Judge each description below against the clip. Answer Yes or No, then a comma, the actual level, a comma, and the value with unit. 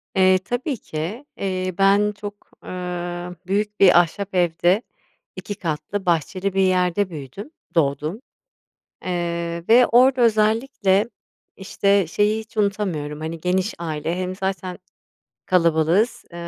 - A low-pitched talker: No, medium, 185 Hz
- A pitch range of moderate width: Yes, average, 3.2 semitones